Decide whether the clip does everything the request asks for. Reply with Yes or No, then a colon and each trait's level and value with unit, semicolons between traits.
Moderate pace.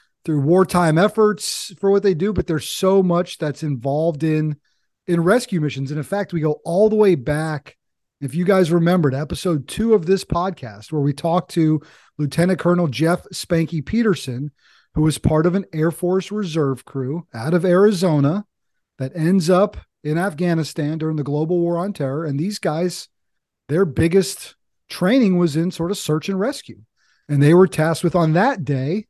Yes: average, 180 wpm